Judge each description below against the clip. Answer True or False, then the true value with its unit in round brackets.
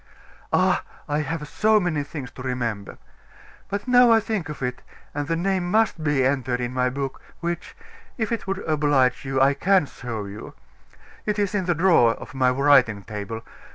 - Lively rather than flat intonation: True (6.6 semitones)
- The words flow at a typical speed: True (185 wpm)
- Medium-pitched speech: True (145 Hz)